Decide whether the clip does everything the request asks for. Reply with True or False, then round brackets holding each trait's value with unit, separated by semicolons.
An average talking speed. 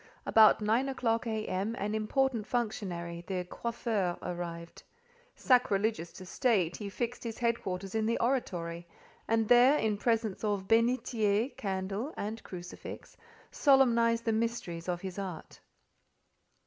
False (130 wpm)